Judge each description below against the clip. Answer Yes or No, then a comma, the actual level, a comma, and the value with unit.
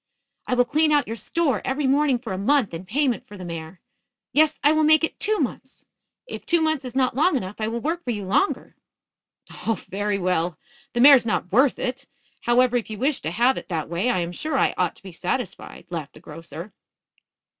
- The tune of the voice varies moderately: No, wide, 7.4 semitones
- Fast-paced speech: Yes, fast, 220 wpm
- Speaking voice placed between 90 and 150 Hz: No, high, 240 Hz